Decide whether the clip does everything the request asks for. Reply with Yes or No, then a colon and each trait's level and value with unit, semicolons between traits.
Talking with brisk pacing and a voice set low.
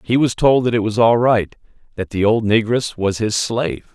Yes: fast, 230 wpm; low, 110 Hz